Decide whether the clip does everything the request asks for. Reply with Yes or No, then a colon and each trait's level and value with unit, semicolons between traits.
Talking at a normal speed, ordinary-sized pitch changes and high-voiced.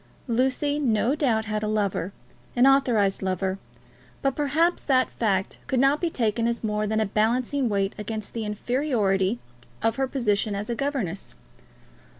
Yes: average, 155 wpm; average, 4.4 semitones; high, 225 Hz